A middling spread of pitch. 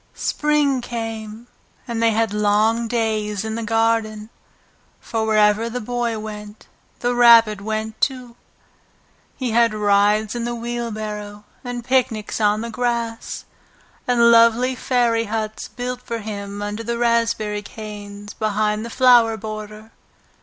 No: narrow, 1.8 semitones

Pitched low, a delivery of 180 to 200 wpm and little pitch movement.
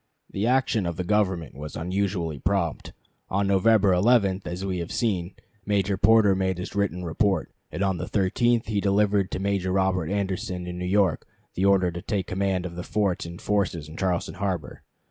Yes: very low, 95 Hz; average, 185 wpm; narrow, 2.1 semitones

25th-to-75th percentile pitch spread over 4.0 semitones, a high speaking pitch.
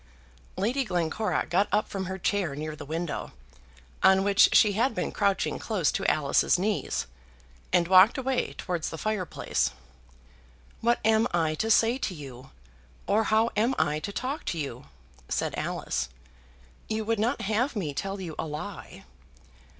Yes: average, 5.3 semitones; high, 195 Hz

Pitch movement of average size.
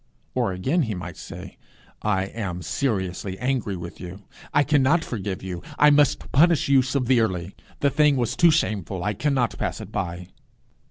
No: wide, 7.0 semitones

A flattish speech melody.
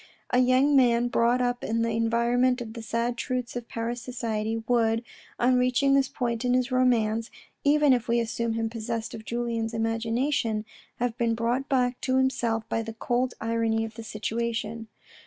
Yes: narrow, 1.7 semitones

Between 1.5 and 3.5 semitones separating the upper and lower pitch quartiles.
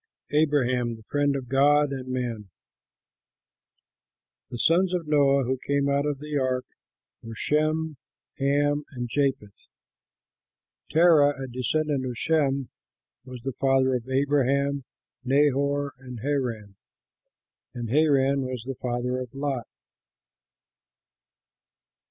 Yes: narrow, 2.4 semitones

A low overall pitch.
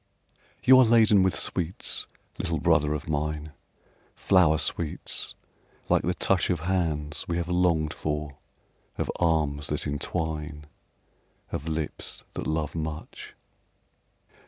Yes: very low, 80 Hz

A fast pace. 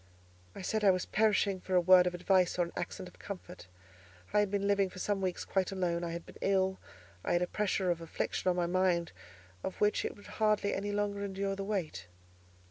Yes: fast, 220 wpm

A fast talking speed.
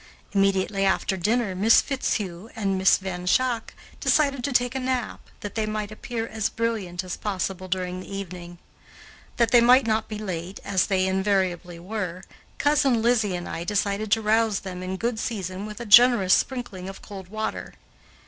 No: average, 175 wpm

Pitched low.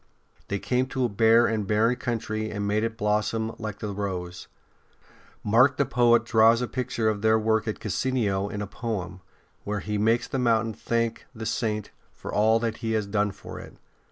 Yes: low, 110 Hz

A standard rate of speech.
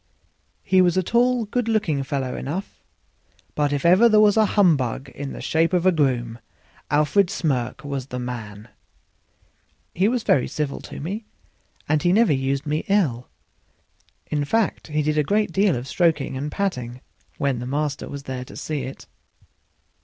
Yes: average, 170 wpm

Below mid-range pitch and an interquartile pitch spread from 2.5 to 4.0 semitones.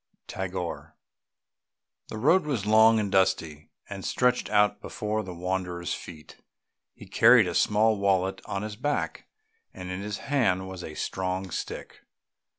Yes: very low, 95 Hz; average, 2.8 semitones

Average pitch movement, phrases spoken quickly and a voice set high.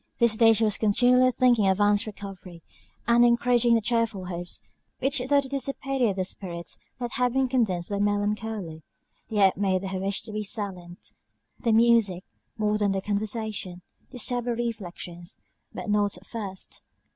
No: average, 3.6 semitones; average, 160 wpm; high, 210 Hz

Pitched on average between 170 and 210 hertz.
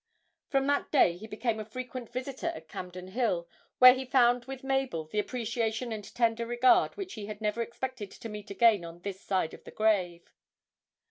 No: high, 225 Hz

